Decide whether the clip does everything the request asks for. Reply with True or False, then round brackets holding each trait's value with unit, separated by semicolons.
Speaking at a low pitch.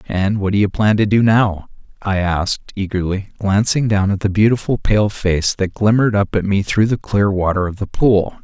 True (100 Hz)